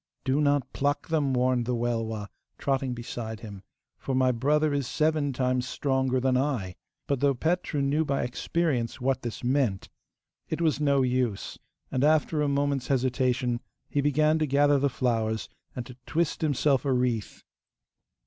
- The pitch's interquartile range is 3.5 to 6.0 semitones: No, average, 2.8 semitones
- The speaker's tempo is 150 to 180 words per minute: Yes, average, 160 wpm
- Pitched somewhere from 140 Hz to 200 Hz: No, low, 130 Hz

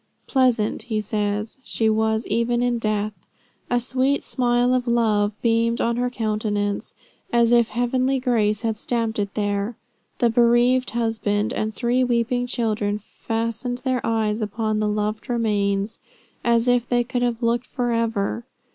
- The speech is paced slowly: No, average, 145 wpm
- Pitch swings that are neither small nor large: No, narrow, 2.3 semitones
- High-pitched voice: Yes, high, 230 Hz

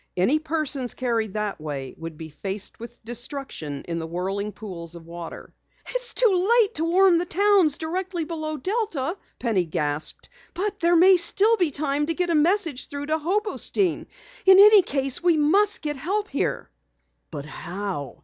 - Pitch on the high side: Yes, very high, 295 Hz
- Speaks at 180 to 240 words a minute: No, average, 170 wpm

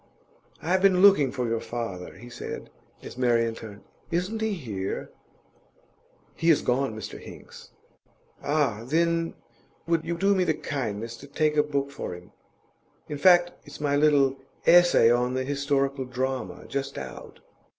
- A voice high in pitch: No, medium, 140 Hz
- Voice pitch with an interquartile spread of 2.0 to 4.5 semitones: No, wide, 5.5 semitones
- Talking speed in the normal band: Yes, average, 155 wpm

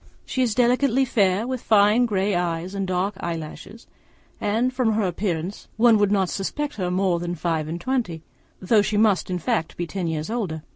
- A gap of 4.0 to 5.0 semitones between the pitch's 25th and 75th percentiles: Yes, average, 4.4 semitones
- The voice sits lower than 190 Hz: No, high, 195 Hz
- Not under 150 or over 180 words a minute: No, average, 190 wpm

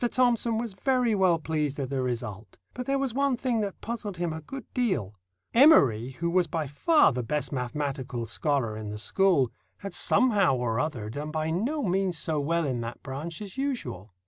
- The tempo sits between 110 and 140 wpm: No, average, 190 wpm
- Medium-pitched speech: Yes, medium, 160 Hz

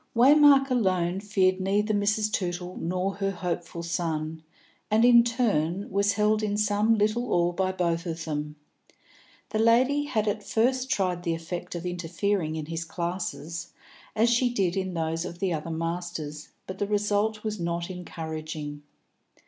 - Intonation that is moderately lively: Yes, average, 4.0 semitones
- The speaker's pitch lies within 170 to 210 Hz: Yes, medium, 185 Hz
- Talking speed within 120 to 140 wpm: No, average, 155 wpm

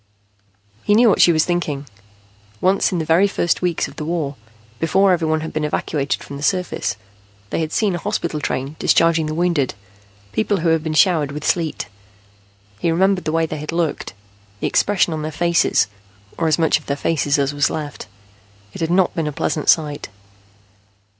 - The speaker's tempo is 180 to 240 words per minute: Yes, average, 190 wpm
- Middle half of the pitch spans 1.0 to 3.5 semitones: Yes, narrow, 2.5 semitones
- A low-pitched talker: No, medium, 160 Hz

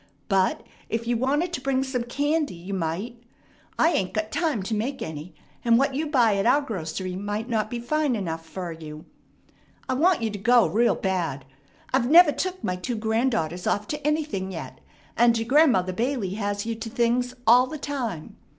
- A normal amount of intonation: No, wide, 5.9 semitones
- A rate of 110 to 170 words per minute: No, average, 190 wpm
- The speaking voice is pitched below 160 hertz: No, high, 230 Hz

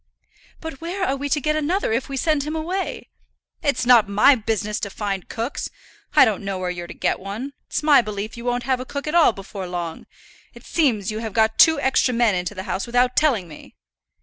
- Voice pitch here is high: Yes, high, 240 Hz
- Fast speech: Yes, fast, 225 wpm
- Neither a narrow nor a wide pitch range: No, wide, 5.9 semitones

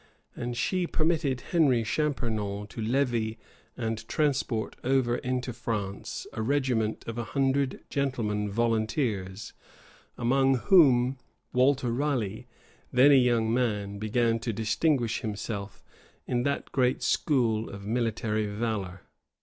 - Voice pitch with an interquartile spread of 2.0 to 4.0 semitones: Yes, average, 3.5 semitones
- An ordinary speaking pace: No, slow, 115 wpm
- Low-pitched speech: Yes, low, 120 Hz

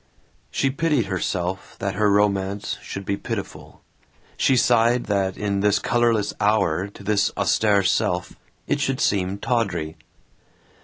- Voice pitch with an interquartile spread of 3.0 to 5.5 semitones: No, narrow, 2.6 semitones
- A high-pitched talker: No, low, 100 Hz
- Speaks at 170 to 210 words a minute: No, slow, 135 wpm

